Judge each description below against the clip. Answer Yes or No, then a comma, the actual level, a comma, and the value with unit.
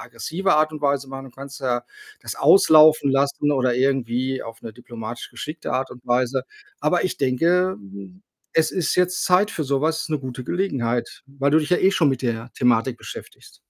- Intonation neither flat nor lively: Yes, average, 4.3 semitones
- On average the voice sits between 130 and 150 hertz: Yes, low, 135 Hz